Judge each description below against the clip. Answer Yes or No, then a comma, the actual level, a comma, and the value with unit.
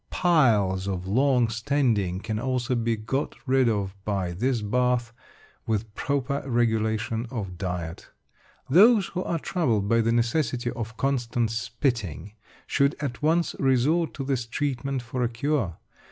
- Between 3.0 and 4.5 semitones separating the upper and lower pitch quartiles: Yes, average, 3.9 semitones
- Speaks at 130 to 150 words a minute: Yes, average, 140 wpm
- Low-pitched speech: Yes, low, 120 Hz